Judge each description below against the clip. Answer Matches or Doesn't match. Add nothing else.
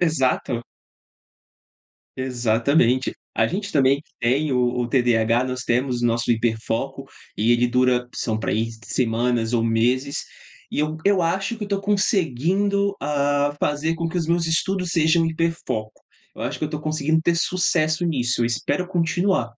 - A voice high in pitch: Doesn't match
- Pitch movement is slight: Doesn't match